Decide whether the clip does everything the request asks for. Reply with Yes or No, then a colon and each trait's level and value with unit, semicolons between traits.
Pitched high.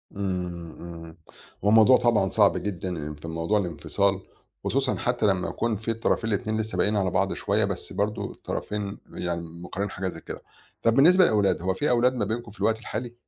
No: low, 100 Hz